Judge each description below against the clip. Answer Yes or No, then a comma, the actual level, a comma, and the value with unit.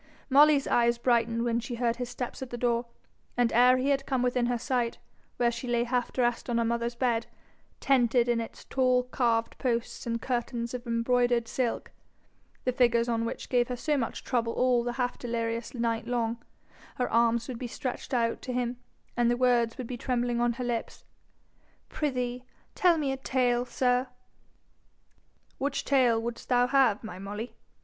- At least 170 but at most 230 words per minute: Yes, average, 180 wpm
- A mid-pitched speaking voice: No, high, 240 Hz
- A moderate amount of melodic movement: No, narrow, 1.3 semitones